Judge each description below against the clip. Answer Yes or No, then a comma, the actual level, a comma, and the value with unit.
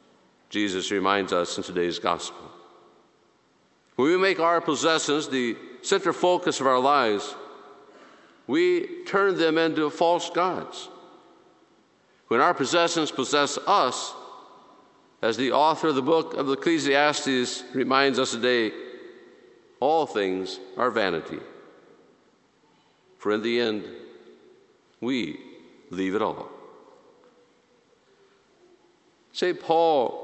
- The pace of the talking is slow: Yes, slow, 105 wpm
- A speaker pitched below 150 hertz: No, medium, 160 Hz